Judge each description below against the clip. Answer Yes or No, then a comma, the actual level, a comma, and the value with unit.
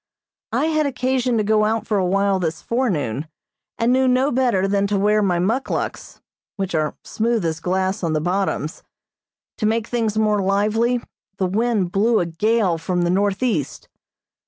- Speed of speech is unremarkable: Yes, average, 170 wpm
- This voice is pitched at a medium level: No, high, 205 Hz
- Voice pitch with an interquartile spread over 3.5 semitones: Yes, average, 4.1 semitones